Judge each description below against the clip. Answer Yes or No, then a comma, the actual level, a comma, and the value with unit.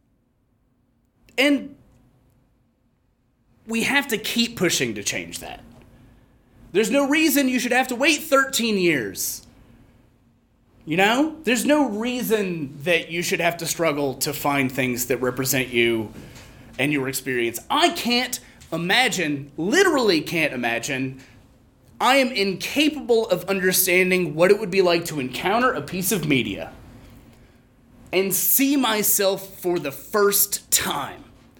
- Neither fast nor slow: No, slow, 130 wpm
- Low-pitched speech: No, medium, 170 Hz